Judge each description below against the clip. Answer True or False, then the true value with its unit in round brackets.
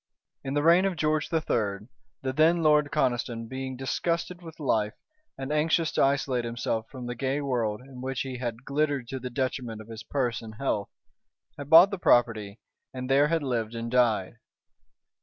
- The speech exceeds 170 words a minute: True (180 wpm)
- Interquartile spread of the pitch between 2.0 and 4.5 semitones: True (4.1 semitones)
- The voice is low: True (130 Hz)